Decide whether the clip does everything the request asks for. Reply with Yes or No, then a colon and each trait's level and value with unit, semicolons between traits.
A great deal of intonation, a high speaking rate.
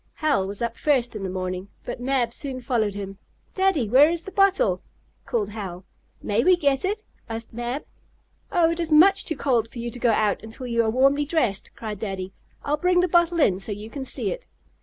Yes: wide, 6.9 semitones; fast, 215 wpm